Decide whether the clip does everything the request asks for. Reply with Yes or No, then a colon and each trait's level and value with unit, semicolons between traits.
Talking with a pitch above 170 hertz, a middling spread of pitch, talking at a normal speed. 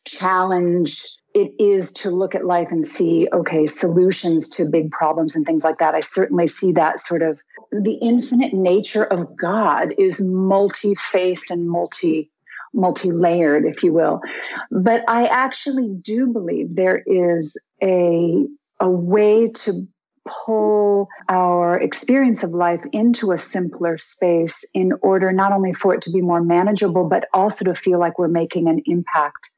Yes: medium, 185 Hz; average, 3.1 semitones; average, 155 wpm